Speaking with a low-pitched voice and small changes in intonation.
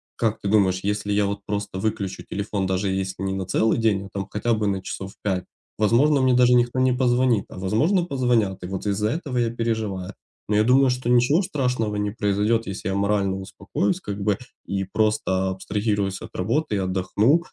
No: low, 105 Hz; average, 3.8 semitones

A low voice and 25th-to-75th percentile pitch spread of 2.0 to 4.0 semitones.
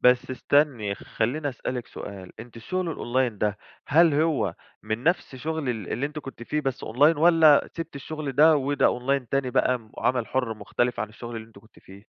No: low, 130 Hz; average, 4.6 semitones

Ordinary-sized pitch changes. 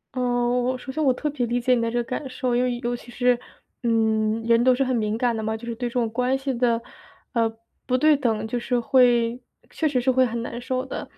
No: narrow, 1.7 semitones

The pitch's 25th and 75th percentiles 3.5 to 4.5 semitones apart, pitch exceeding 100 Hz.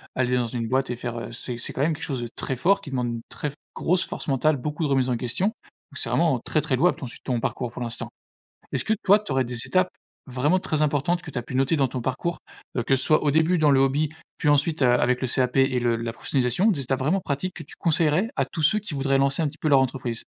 Yes: average, 3.8 semitones; low, 135 Hz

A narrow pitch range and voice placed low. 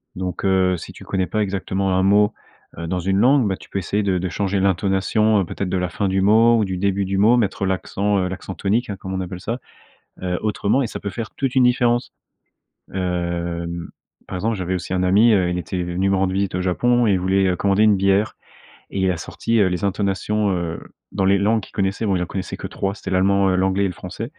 Yes: narrow, 2.0 semitones; very low, 95 Hz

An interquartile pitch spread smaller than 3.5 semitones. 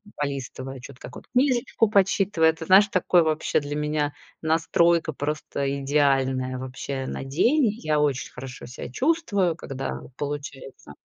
No: average, 4.2 semitones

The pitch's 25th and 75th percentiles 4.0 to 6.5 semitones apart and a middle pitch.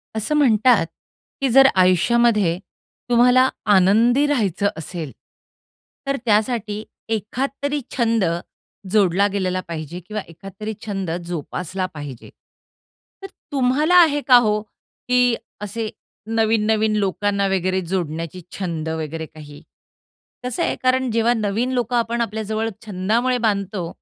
No: average, 4.5 semitones; high, 215 Hz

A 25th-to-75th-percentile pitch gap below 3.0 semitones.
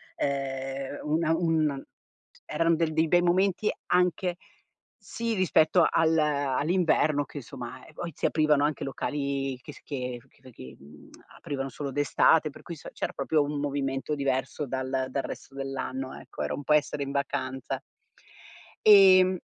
No: average, 3.3 semitones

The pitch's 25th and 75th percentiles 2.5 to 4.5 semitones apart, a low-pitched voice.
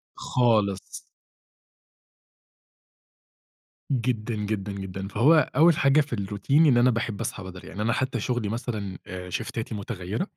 Yes: average, 3.8 semitones; low, 110 Hz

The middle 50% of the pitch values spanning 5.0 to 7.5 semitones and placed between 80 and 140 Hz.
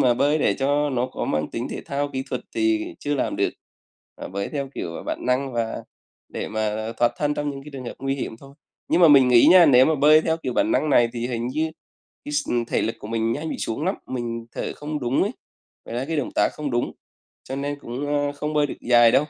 No: average, 3.7 semitones; low, 135 Hz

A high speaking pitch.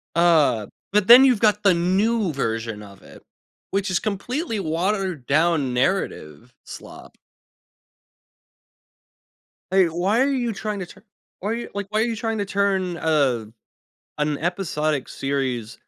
No: medium, 180 Hz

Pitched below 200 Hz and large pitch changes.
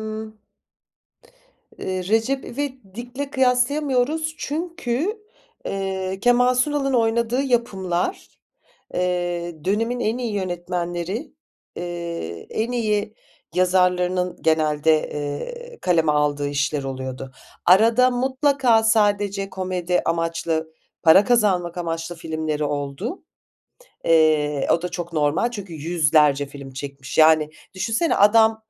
Yes: medium, 185 Hz; wide, 6.9 semitones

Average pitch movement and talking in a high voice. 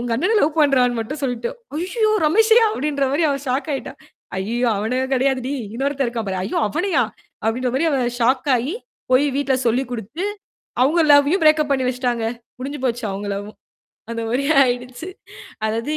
Yes: average, 3.5 semitones; very high, 260 Hz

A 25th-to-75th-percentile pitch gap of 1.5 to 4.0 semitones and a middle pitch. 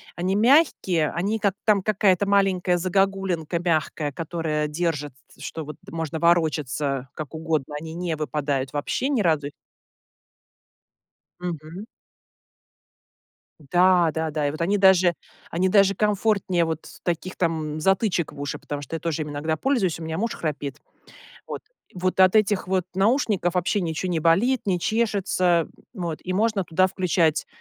Yes: average, 3.6 semitones; medium, 175 Hz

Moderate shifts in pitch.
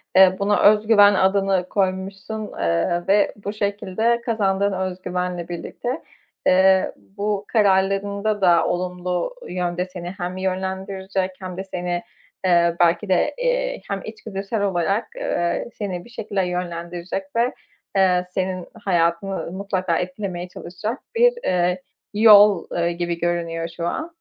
No: narrow, 2.3 semitones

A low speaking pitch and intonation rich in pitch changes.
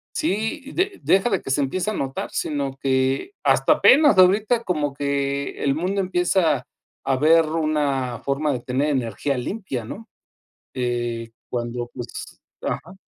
No: medium, 145 Hz; wide, 6.1 semitones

